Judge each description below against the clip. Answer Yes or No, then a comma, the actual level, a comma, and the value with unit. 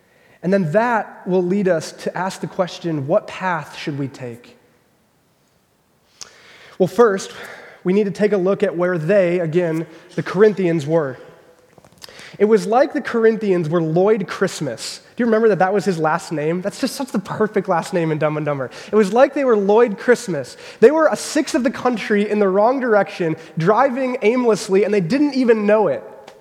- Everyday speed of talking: Yes, average, 190 wpm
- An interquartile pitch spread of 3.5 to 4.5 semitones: Yes, average, 4.2 semitones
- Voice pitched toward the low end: No, high, 200 Hz